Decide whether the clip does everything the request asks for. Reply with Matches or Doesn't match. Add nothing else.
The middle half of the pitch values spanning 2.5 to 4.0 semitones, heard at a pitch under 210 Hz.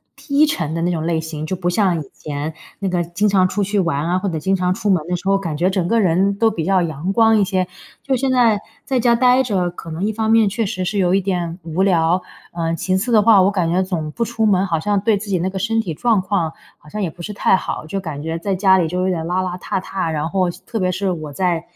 Matches